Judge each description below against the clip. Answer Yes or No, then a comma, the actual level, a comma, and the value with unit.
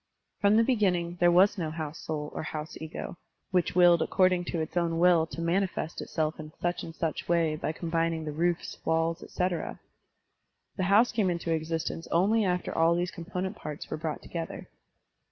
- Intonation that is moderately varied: No, narrow, 1.9 semitones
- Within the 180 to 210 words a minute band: Yes, average, 185 wpm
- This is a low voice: No, medium, 170 Hz